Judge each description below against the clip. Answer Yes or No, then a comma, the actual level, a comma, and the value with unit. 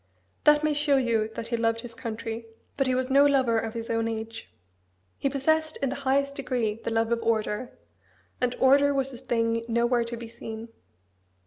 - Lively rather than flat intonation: No, average, 3.0 semitones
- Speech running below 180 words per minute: No, average, 195 wpm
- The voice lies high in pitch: Yes, high, 235 Hz